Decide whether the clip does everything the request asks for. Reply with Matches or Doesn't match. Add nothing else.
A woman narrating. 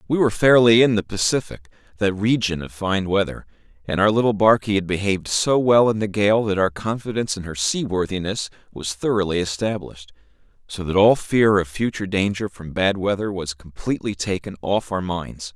Doesn't match